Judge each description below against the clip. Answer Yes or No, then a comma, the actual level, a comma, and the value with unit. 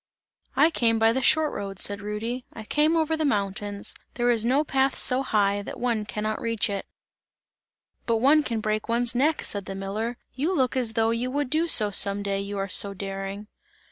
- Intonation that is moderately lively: Yes, average, 4.3 semitones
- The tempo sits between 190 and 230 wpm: Yes, fast, 205 wpm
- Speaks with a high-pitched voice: Yes, high, 225 Hz